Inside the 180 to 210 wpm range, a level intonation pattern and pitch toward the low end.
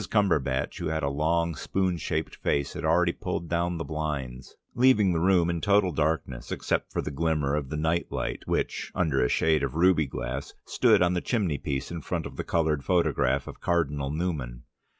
No: average, 190 wpm; average, 3.4 semitones; very low, 80 Hz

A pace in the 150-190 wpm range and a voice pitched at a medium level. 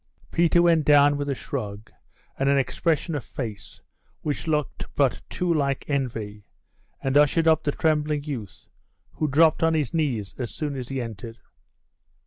Yes: average, 160 wpm; medium, 145 Hz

